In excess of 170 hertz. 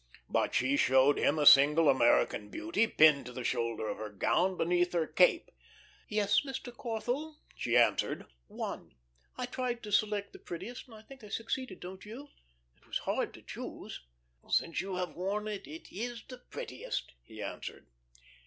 Yes: high, 190 Hz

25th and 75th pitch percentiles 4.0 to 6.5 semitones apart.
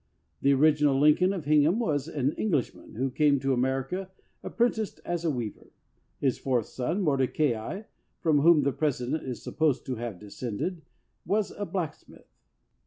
Yes: average, 4.4 semitones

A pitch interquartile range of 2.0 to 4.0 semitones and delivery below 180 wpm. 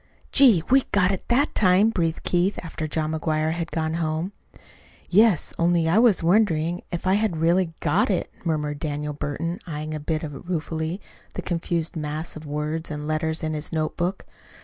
Yes: average, 2.7 semitones; average, 170 wpm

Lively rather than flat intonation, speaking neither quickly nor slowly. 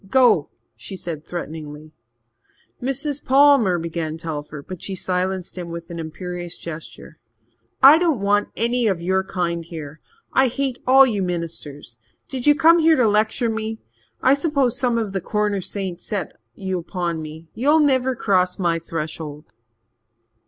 Yes: wide, 6.9 semitones; average, 150 wpm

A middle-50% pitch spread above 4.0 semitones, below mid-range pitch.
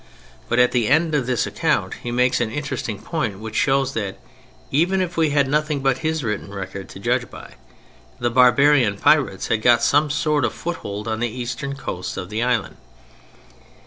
Yes: average, 4.9 semitones; low, 125 Hz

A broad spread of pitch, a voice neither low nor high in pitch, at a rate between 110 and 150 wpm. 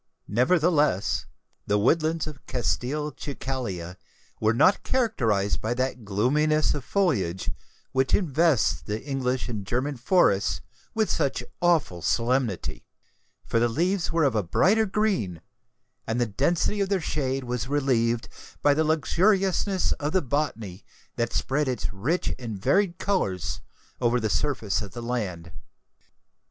No: wide, 6.4 semitones; low, 130 Hz; slow, 135 wpm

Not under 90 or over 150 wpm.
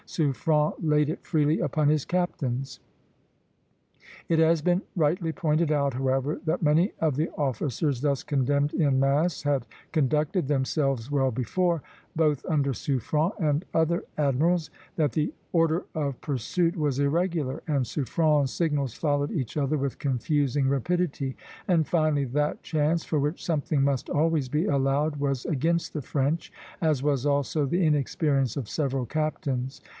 Yes: average, 145 wpm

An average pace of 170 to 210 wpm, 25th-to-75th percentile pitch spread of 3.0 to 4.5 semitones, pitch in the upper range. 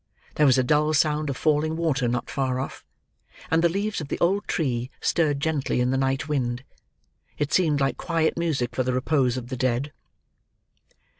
No: average, 190 wpm; average, 3.6 semitones; medium, 145 Hz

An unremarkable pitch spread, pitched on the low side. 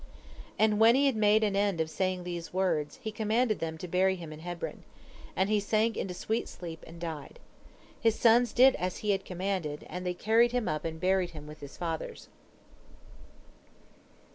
No: average, 4.5 semitones; high, 190 Hz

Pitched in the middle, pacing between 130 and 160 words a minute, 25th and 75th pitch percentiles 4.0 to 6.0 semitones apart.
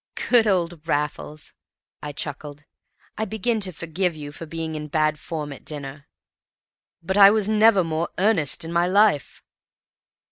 Yes: medium, 165 Hz; average, 150 wpm; average, 4.6 semitones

